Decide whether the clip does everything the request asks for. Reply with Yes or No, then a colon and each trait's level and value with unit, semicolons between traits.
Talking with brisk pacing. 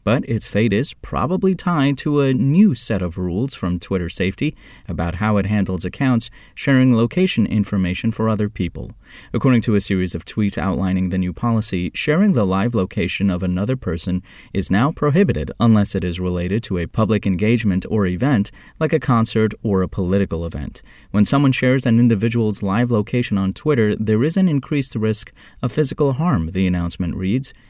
No: average, 180 wpm